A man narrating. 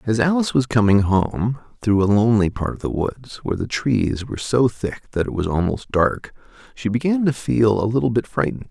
Yes: male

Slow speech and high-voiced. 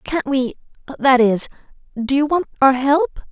Yes: slow, 125 wpm; very high, 270 Hz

